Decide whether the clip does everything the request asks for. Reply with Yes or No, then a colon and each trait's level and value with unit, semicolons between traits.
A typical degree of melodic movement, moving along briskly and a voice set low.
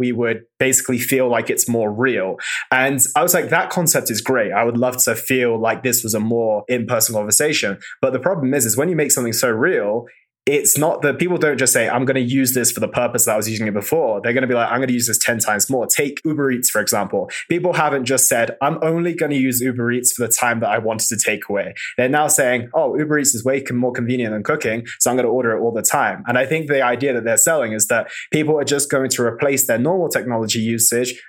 Yes: average, 3.4 semitones; fast, 260 wpm; low, 125 Hz